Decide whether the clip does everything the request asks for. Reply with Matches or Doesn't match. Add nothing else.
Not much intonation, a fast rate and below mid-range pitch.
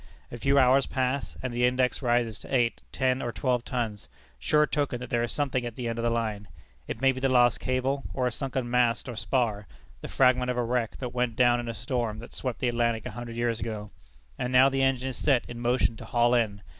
Matches